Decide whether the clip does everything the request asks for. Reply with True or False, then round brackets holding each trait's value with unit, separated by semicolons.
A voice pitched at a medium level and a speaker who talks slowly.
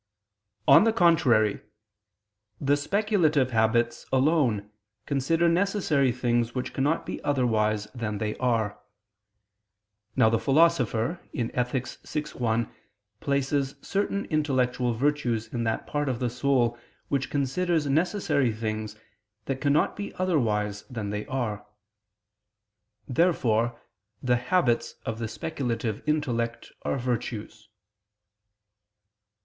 False (125 Hz; 110 wpm)